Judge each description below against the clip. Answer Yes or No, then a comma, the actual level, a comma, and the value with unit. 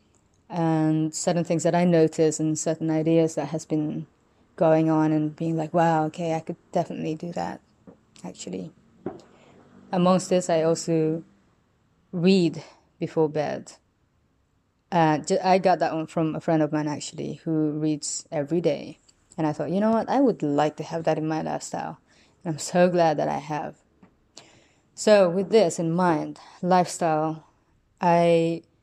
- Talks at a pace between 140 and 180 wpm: Yes, average, 160 wpm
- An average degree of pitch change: No, narrow, 1.9 semitones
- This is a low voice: No, medium, 160 Hz